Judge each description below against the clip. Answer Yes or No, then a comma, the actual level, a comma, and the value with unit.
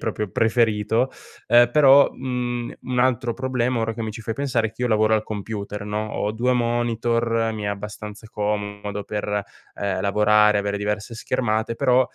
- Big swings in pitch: No, narrow, 2.5 semitones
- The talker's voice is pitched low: Yes, low, 110 Hz